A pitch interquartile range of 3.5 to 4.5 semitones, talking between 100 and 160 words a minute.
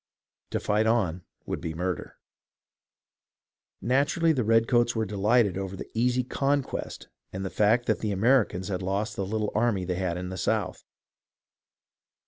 Yes: average, 4.1 semitones; average, 150 wpm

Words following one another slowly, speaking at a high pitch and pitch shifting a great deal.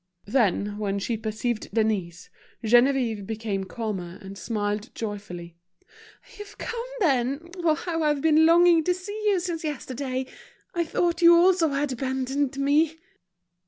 Yes: slow, 130 wpm; very high, 265 Hz; wide, 7.4 semitones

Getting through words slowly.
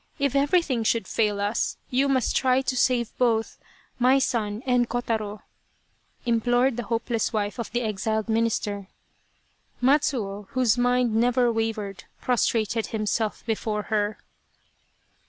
Yes: slow, 130 wpm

